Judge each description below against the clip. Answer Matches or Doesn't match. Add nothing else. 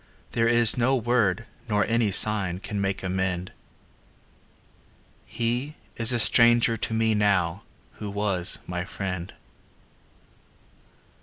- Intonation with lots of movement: Doesn't match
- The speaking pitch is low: Matches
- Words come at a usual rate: Doesn't match